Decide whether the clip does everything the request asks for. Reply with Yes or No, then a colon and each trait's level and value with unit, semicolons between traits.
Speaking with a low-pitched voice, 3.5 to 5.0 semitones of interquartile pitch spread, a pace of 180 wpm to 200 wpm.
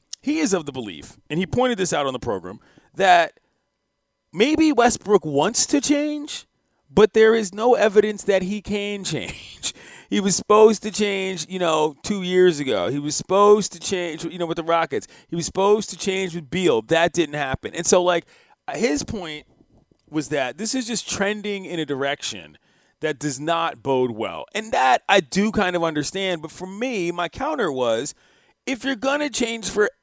No: high, 190 Hz; average, 4.3 semitones; average, 190 wpm